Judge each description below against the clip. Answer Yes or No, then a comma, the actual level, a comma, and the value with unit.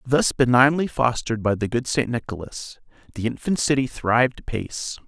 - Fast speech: No, average, 155 wpm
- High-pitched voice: No, low, 125 Hz